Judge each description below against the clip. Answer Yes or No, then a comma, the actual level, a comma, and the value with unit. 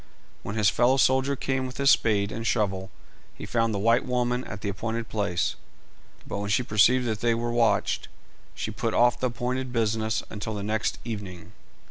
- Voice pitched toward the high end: No, low, 115 Hz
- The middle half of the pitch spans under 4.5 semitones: Yes, average, 3.1 semitones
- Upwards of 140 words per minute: Yes, average, 180 wpm